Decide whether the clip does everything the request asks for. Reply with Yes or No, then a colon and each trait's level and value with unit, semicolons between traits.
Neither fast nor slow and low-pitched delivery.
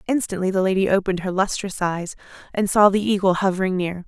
No: average, 190 wpm; high, 190 Hz